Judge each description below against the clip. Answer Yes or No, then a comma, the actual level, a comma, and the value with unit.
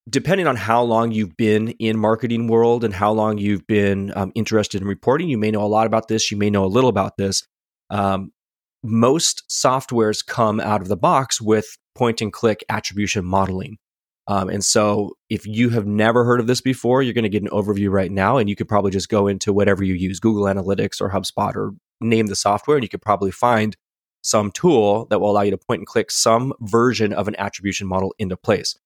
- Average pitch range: No, narrow, 2.3 semitones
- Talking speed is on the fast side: Yes, fast, 220 wpm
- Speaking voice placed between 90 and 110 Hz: Yes, low, 105 Hz